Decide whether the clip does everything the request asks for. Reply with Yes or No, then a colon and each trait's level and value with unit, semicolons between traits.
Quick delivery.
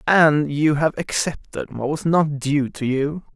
No: average, 180 wpm